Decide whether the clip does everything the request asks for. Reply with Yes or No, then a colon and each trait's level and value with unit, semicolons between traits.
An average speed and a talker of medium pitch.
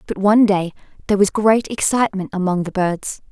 No: average, 180 wpm; high, 200 Hz